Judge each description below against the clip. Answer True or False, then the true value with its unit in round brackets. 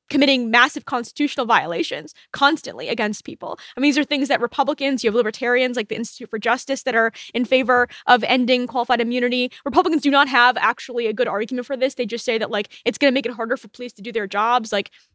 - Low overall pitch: False (245 Hz)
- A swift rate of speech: True (230 wpm)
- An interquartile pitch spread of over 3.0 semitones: False (2.5 semitones)